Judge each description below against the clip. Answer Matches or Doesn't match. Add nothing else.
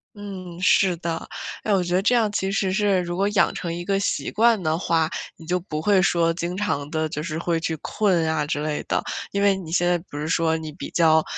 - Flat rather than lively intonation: Doesn't match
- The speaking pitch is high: Doesn't match